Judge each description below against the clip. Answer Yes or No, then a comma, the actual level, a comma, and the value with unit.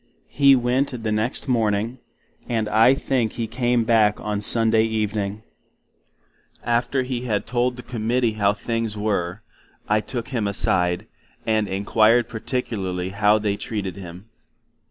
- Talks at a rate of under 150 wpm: Yes, average, 140 wpm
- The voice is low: Yes, low, 110 Hz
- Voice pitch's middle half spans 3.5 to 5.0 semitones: No, narrow, 2.6 semitones